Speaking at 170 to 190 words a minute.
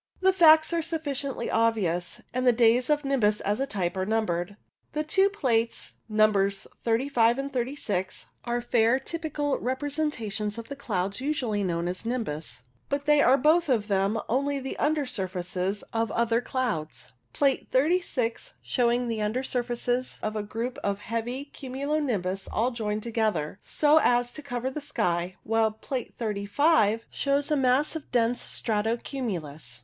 No: average, 155 wpm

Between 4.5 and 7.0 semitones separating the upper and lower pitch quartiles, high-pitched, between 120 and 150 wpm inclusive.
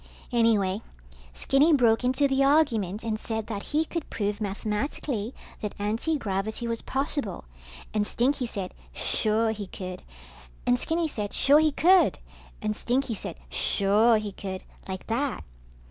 Yes: average, 4.9 semitones; high, 225 Hz; average, 140 wpm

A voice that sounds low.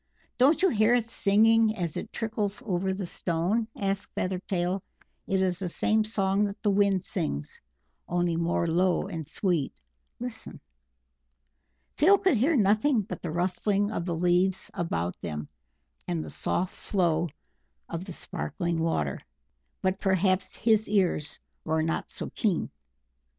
No: high, 190 Hz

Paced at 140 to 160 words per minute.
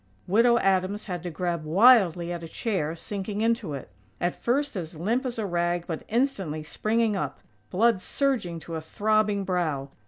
No: average, 180 wpm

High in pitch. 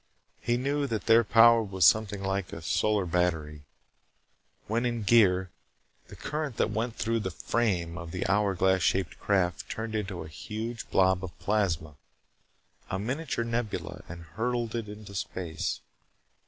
No: low, 105 Hz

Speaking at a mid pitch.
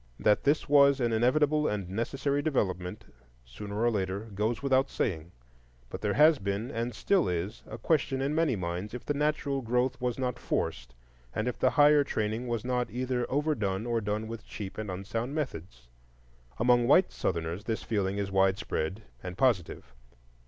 No: low, 115 Hz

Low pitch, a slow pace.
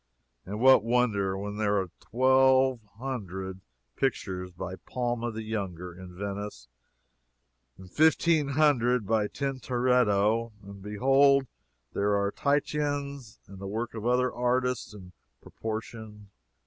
Yes: low, 115 Hz; slow, 120 wpm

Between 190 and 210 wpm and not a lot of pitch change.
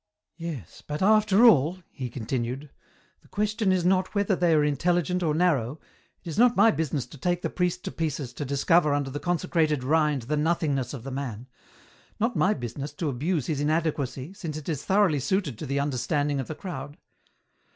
No: average, 200 wpm; average, 4.4 semitones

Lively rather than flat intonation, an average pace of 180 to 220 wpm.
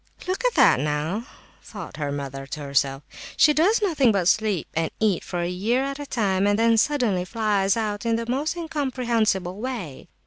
Yes: wide, 6.6 semitones; average, 185 wpm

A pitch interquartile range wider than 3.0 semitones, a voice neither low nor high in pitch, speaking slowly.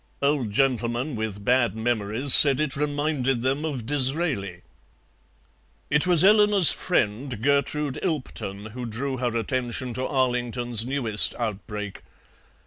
No: average, 4.0 semitones; low, 130 Hz; slow, 120 wpm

